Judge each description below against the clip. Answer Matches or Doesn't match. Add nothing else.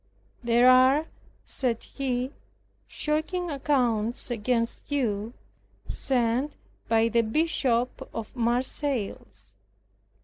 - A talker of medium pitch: Doesn't match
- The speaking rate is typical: Doesn't match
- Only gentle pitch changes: Doesn't match